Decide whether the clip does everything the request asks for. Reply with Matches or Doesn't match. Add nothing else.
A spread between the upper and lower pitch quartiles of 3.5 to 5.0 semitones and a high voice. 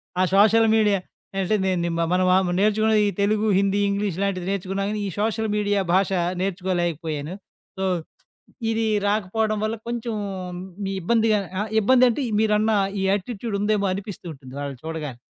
Doesn't match